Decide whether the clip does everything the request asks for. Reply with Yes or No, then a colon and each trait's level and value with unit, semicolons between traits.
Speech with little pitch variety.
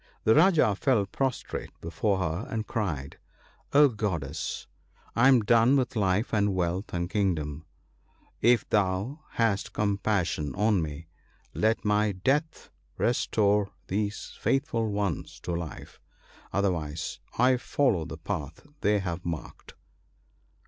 No: average, 4.7 semitones